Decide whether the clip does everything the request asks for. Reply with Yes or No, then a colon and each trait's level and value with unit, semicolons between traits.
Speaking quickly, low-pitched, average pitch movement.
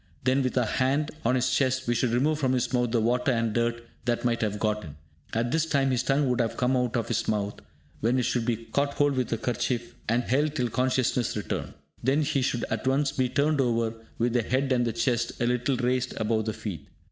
No: fast, 240 wpm; low, 125 Hz; narrow, 2.2 semitones